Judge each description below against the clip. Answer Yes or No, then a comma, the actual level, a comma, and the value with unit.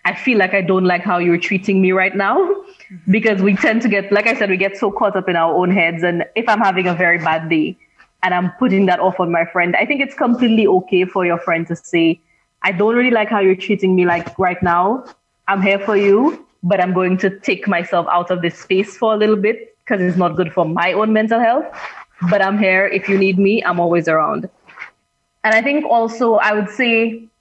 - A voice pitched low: No, high, 195 Hz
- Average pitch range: Yes, average, 3.3 semitones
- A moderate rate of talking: No, fast, 240 wpm